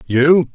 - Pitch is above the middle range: No, medium, 145 Hz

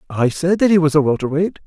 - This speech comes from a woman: No, male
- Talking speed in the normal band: No, fast, 290 wpm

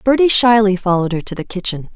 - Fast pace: Yes, fast, 215 wpm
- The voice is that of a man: No, female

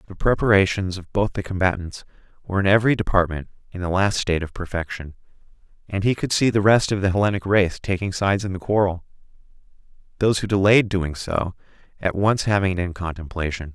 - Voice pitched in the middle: No, very low, 95 Hz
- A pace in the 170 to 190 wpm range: Yes, average, 185 wpm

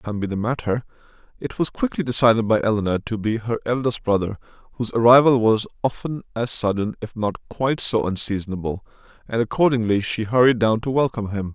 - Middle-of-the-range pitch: No, low, 115 Hz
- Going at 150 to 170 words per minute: No, average, 180 wpm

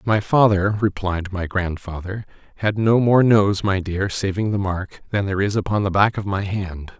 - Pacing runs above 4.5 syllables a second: Yes, 4.7 syllables/s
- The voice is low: Yes, low, 100 Hz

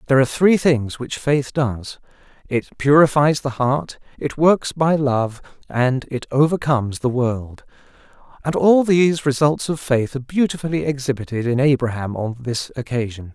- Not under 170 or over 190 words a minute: No, average, 155 wpm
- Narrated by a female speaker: No, male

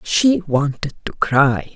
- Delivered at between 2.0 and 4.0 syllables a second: Yes, 3.4 syllables/s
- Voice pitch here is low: No, medium, 155 Hz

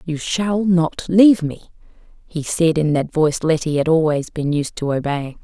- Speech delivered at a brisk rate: No, average, 190 wpm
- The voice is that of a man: No, female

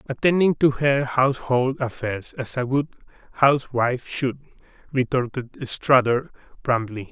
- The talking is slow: Yes, slow, 110 wpm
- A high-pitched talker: No, low, 130 Hz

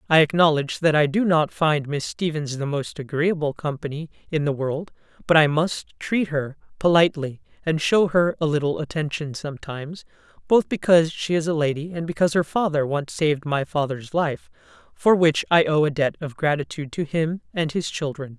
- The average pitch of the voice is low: No, medium, 155 Hz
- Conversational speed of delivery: Yes, average, 185 wpm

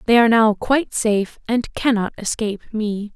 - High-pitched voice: Yes, high, 220 Hz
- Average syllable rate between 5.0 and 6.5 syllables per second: Yes, 5.7 syllables/s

